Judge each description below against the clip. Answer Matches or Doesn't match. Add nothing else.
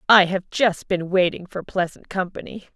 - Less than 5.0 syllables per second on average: Matches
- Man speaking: Doesn't match